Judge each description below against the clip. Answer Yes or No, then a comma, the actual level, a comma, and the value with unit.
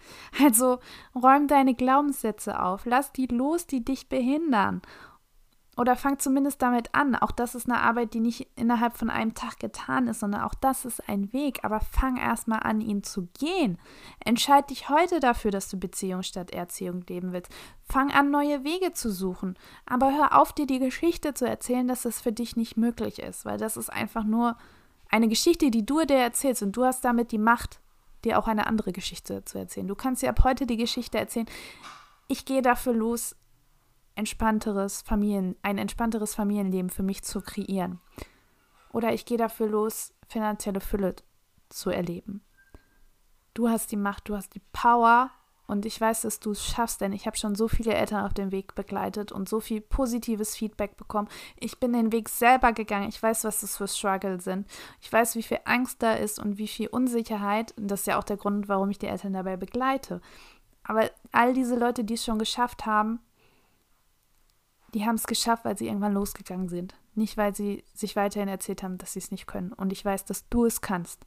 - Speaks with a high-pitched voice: Yes, high, 220 Hz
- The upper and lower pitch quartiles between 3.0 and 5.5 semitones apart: Yes, average, 3.5 semitones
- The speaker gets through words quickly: Yes, fast, 200 wpm